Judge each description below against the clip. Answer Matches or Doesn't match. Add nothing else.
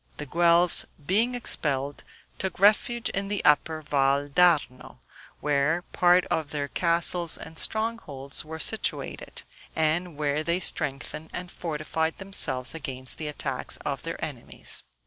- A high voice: Doesn't match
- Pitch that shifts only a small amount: Doesn't match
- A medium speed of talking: Doesn't match